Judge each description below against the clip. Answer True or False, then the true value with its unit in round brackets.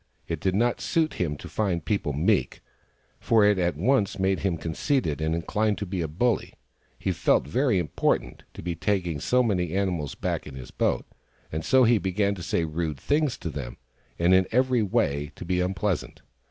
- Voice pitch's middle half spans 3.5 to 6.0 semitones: True (4.7 semitones)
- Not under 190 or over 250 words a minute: True (195 wpm)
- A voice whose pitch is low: True (95 Hz)